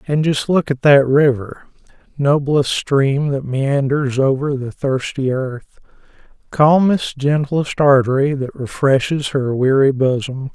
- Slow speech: Yes, slow, 115 wpm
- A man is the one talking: Yes, male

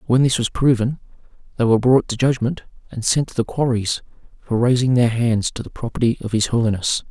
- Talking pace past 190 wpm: Yes, fast, 205 wpm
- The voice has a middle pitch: No, low, 120 Hz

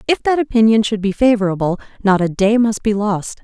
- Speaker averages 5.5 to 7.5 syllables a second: Yes, 5.6 syllables/s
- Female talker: Yes, female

